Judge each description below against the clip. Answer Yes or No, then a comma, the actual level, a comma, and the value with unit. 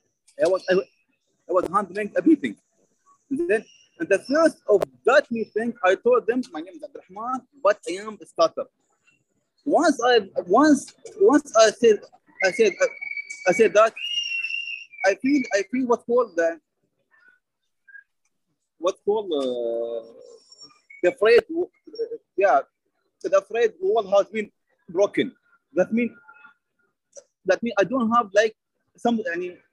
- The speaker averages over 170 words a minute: No, average, 145 wpm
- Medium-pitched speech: No, very high, 270 Hz